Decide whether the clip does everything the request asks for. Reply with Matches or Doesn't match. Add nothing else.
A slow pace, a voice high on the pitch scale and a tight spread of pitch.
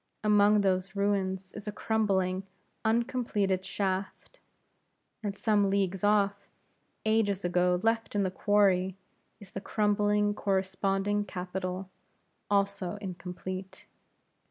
Matches